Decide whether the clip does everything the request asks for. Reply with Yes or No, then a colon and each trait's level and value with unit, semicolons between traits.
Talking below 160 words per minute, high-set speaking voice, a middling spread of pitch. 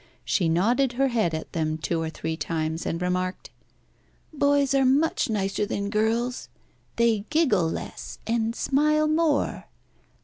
No: average, 140 wpm; high, 220 Hz; wide, 7.8 semitones